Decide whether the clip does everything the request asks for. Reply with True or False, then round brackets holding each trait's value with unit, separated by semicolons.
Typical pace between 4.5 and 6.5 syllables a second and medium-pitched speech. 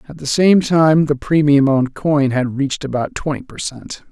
True (4.6 syllables/s; 145 Hz)